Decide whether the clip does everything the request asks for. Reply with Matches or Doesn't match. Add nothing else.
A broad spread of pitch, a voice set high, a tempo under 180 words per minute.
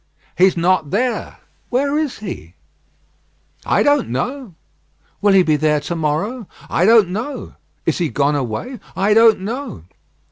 Matches